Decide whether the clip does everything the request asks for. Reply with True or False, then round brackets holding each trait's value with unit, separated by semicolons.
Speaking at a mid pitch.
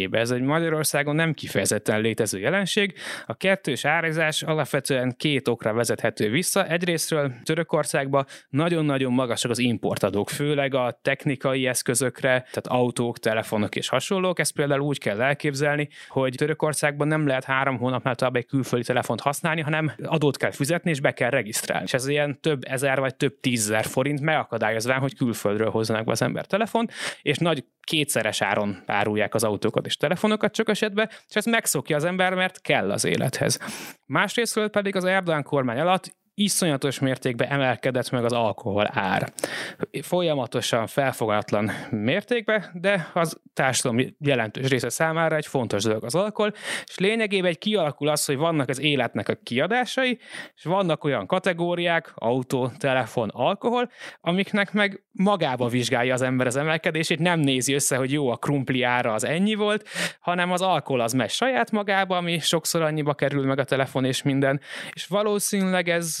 True (145 Hz)